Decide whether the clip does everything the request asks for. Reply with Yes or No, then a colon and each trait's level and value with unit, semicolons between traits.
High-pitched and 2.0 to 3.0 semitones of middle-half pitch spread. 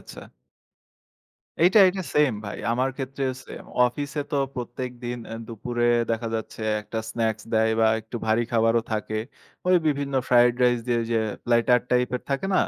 No: low, 120 Hz; average, 2.7 semitones